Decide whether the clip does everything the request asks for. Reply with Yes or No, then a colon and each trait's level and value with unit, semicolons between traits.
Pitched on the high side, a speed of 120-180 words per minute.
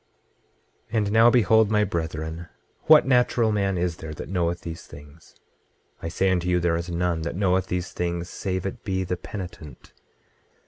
No: very low, 90 Hz; average, 175 wpm